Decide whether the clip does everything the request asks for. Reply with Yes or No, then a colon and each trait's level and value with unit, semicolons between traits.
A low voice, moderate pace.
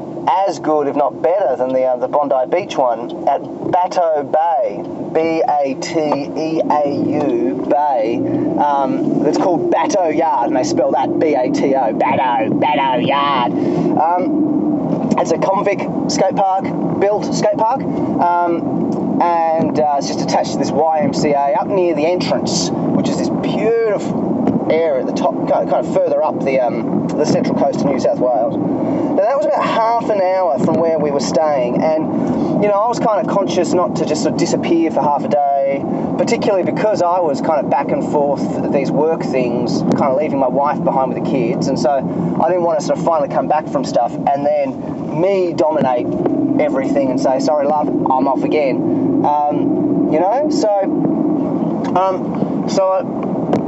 No: high, 225 Hz; average, 180 wpm